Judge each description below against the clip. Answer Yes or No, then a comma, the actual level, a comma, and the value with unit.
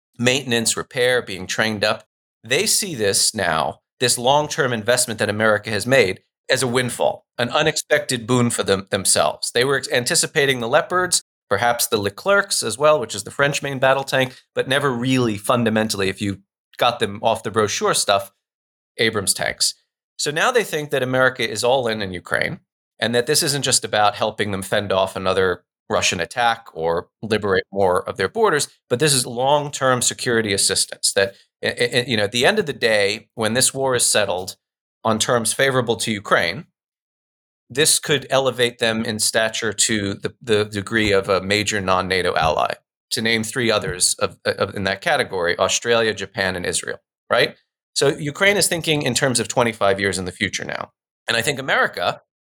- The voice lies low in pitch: Yes, low, 120 Hz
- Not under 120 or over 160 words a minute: No, average, 185 wpm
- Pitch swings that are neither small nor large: Yes, average, 4.6 semitones